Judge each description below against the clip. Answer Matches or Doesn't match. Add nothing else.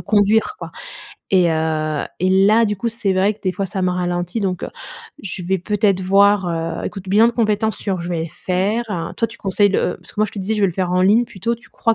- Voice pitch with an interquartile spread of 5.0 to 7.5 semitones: Doesn't match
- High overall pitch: Matches